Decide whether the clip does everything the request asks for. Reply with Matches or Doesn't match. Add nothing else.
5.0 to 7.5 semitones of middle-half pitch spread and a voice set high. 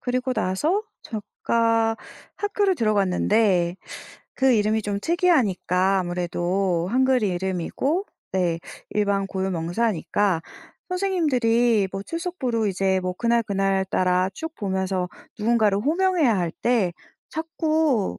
Matches